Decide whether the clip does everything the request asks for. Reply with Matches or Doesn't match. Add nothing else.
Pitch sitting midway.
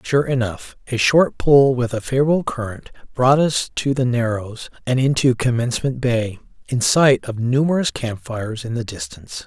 Doesn't match